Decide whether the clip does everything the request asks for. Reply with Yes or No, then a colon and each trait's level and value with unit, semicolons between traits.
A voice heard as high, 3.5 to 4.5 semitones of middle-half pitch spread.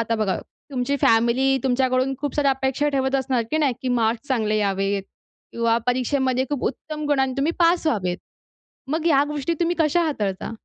Yes: very high, 265 Hz; average, 3.9 semitones